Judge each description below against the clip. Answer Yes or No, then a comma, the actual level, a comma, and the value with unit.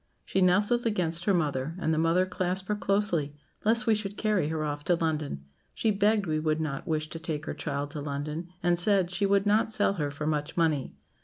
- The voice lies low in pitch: No, medium, 170 Hz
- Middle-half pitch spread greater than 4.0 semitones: Yes, average, 4.5 semitones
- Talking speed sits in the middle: No, fast, 220 wpm